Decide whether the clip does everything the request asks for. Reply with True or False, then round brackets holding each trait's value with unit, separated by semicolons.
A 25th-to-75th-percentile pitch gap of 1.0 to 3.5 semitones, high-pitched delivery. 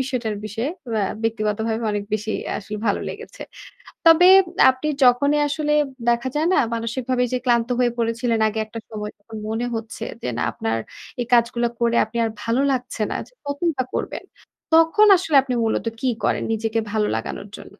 True (2.9 semitones; 235 Hz)